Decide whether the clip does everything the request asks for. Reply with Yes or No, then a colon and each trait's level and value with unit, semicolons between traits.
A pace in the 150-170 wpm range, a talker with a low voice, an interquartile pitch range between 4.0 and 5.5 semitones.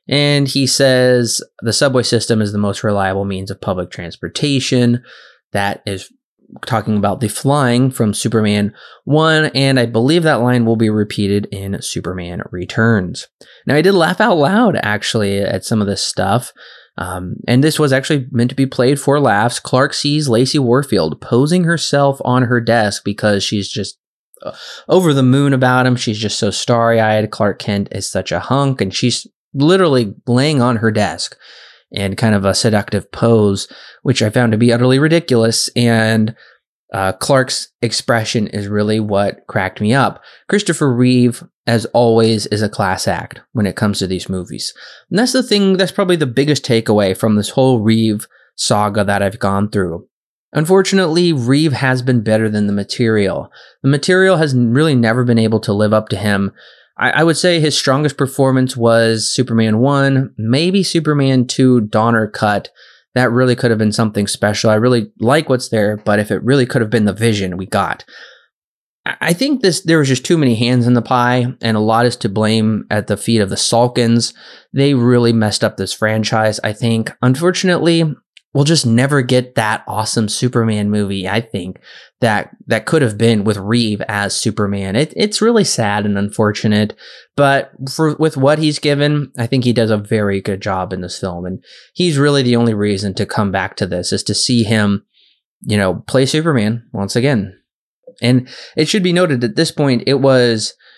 No: average, 185 wpm; low, 115 Hz; average, 4.4 semitones